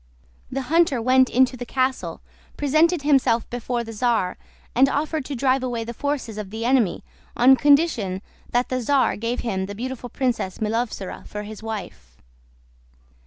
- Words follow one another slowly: No, average, 160 wpm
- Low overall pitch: No, high, 245 Hz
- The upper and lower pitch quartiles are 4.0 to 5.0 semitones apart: No, average, 3.3 semitones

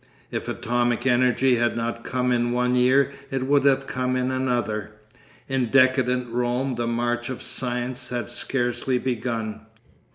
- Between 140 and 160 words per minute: Yes, average, 150 wpm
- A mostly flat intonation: Yes, narrow, 1.3 semitones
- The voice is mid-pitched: No, low, 125 Hz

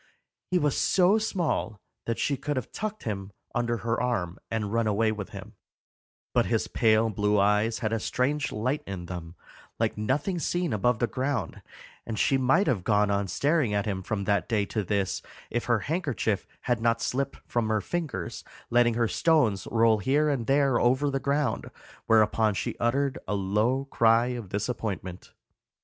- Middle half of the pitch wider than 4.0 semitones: Yes, average, 4.7 semitones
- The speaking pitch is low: Yes, low, 115 Hz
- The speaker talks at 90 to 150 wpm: No, average, 175 wpm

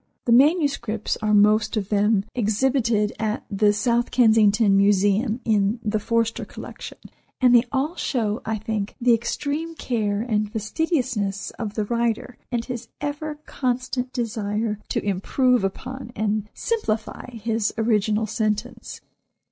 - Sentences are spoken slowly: Yes, slow, 130 wpm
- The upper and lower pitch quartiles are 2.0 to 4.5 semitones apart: Yes, average, 2.9 semitones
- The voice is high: Yes, high, 225 Hz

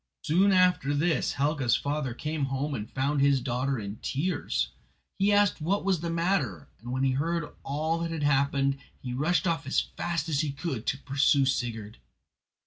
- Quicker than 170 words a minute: Yes, average, 180 wpm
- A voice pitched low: No, medium, 145 Hz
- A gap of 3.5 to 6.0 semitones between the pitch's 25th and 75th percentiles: Yes, average, 3.8 semitones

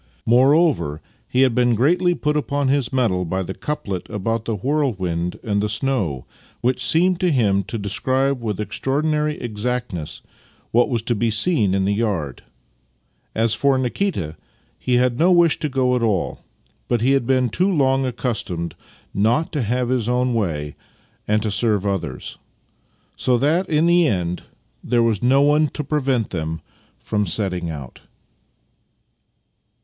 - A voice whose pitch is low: Yes, low, 120 Hz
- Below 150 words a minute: No, average, 160 wpm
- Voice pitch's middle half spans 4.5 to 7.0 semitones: Yes, wide, 5.4 semitones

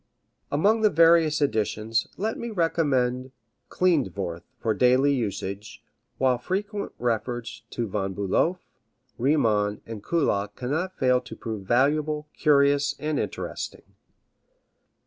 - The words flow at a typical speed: No, slow, 110 wpm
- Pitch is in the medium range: No, low, 130 Hz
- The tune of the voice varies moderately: No, wide, 5.8 semitones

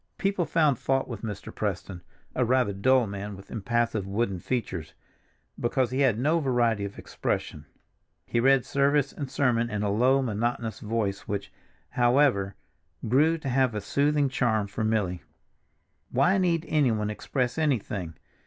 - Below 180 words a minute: Yes, average, 145 wpm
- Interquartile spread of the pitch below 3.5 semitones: No, average, 4.7 semitones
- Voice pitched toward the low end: Yes, low, 120 Hz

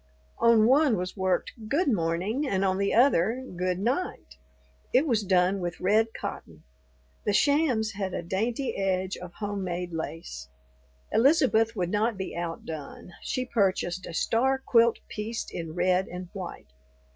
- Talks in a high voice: Yes, high, 200 Hz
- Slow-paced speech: No, average, 145 wpm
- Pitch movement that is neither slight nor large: Yes, average, 4.5 semitones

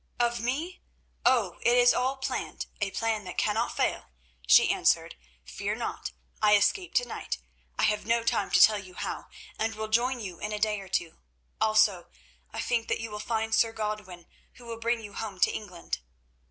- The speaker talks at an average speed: Yes, average, 185 wpm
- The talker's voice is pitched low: No, high, 220 Hz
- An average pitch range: No, narrow, 2.2 semitones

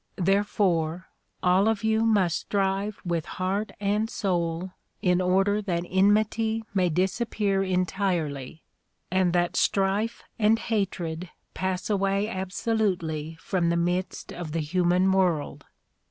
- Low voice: No, high, 190 Hz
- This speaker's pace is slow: Yes, slow, 125 wpm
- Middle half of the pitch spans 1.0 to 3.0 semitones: Yes, average, 2.7 semitones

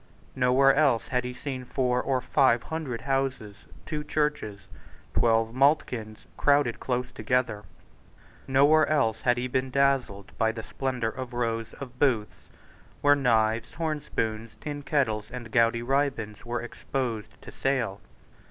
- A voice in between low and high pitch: No, low, 125 Hz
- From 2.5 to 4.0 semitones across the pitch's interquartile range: Yes, average, 3.3 semitones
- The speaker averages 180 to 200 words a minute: No, average, 140 wpm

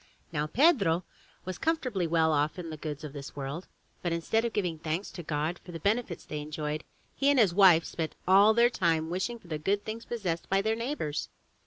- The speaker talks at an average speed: No, fast, 215 wpm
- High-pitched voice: No, medium, 175 Hz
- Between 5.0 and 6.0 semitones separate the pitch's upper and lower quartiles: Yes, wide, 5.6 semitones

